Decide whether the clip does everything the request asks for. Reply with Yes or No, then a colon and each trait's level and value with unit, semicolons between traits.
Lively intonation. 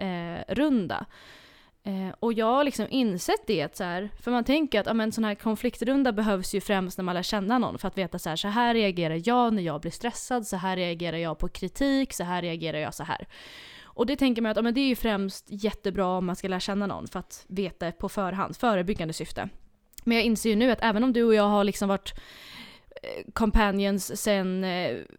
No: average, 4.0 semitones